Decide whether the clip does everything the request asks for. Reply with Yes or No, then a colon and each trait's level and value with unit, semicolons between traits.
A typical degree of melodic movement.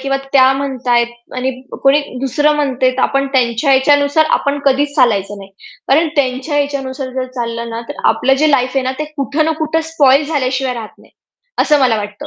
No: narrow, 2.3 semitones